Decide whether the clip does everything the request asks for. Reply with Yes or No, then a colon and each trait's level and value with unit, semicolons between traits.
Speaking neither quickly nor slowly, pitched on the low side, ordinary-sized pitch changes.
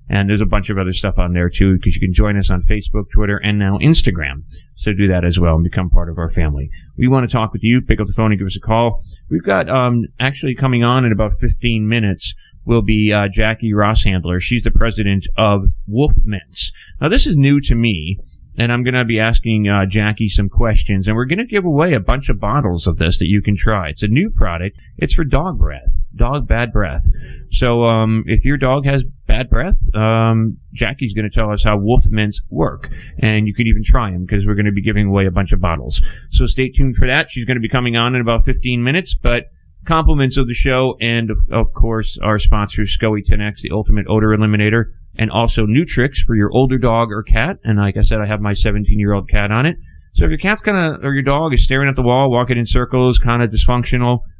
No: fast, 245 wpm; low, 110 Hz; average, 3.7 semitones